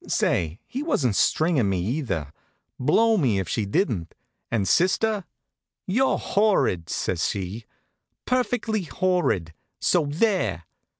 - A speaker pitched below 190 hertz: Yes, medium, 140 Hz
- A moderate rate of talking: No, slow, 115 wpm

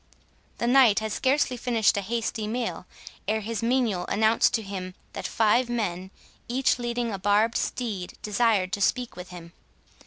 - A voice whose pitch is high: Yes, high, 220 Hz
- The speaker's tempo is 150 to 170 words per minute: Yes, average, 160 wpm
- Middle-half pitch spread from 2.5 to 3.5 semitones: Yes, average, 3.1 semitones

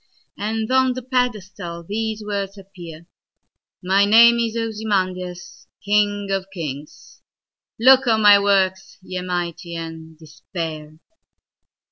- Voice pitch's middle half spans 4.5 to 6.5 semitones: No, average, 4.0 semitones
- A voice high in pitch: Yes, high, 195 Hz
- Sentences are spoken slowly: Yes, slow, 100 wpm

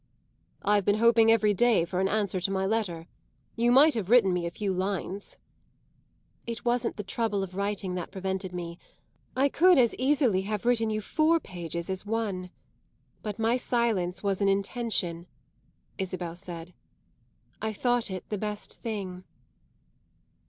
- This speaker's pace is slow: No, average, 155 wpm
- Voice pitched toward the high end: Yes, high, 205 Hz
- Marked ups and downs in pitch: No, average, 3.6 semitones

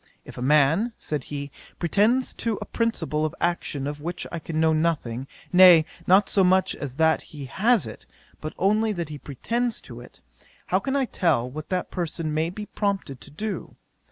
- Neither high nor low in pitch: Yes, medium, 165 Hz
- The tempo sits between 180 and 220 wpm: Yes, average, 190 wpm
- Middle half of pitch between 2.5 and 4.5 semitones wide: No, average, 5.3 semitones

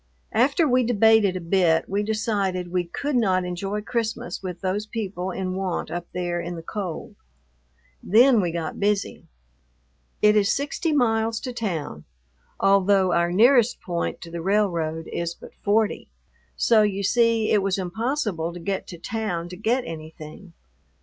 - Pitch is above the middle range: Yes, high, 195 Hz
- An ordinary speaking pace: Yes, average, 155 wpm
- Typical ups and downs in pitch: Yes, average, 4.1 semitones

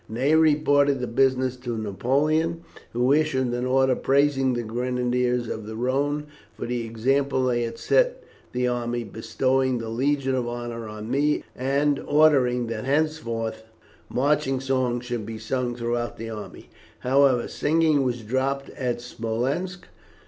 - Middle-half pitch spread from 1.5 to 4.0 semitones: Yes, average, 2.9 semitones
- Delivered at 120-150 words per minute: Yes, average, 145 wpm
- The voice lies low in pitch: Yes, low, 125 Hz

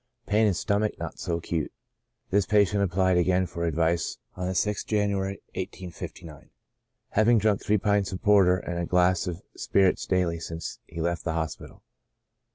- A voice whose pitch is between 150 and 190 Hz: No, very low, 95 Hz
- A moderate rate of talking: Yes, average, 165 wpm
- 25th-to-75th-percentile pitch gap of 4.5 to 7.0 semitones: No, average, 3.0 semitones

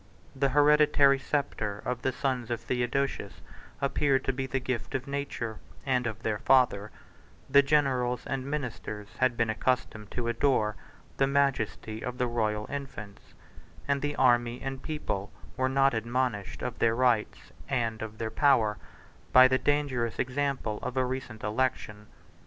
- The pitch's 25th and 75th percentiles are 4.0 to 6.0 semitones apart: No, average, 3.4 semitones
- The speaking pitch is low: Yes, low, 125 Hz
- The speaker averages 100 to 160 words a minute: Yes, average, 150 wpm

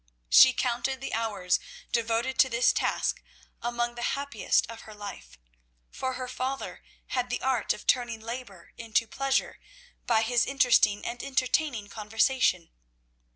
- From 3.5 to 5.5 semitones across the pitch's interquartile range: No, average, 2.7 semitones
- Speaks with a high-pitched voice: Yes, high, 240 Hz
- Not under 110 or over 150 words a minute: Yes, average, 140 wpm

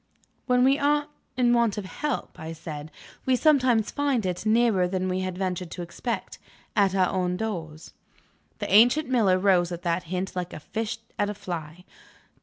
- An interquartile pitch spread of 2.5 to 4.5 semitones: No, average, 5.1 semitones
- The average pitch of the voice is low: No, high, 190 Hz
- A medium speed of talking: Yes, average, 180 wpm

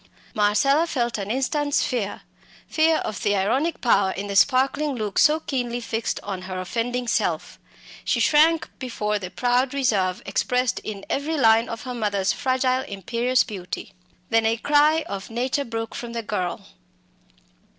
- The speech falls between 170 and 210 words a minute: No, average, 155 wpm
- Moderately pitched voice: No, high, 235 Hz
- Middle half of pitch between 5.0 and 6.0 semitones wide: No, average, 4.4 semitones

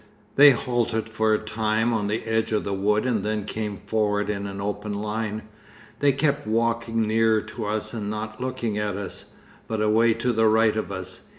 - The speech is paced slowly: No, average, 195 wpm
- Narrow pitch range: Yes, narrow, 1.3 semitones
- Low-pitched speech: Yes, low, 110 Hz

